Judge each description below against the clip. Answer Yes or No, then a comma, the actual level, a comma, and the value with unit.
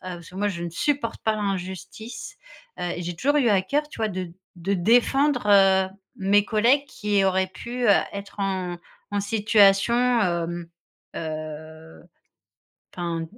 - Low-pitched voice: No, high, 195 Hz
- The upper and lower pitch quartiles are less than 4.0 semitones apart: No, average, 4.3 semitones